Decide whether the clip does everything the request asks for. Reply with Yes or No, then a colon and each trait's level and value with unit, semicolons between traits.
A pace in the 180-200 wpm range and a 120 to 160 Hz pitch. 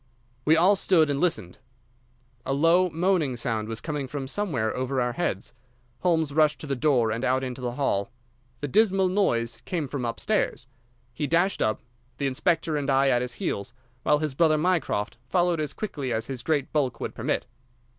Yes: average, 185 wpm; medium, 140 Hz